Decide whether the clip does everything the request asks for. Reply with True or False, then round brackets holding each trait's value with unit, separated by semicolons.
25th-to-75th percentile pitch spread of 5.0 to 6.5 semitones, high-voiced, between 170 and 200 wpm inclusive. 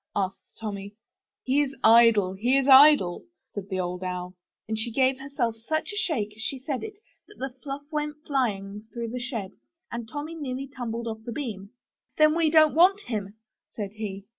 True (5.6 semitones; 235 Hz; 190 wpm)